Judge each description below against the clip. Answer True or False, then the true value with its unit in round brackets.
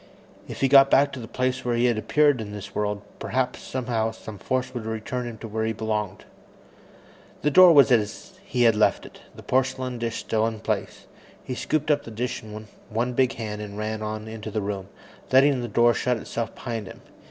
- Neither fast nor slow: False (210 wpm)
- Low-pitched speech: True (115 Hz)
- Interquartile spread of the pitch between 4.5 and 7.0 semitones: False (2.9 semitones)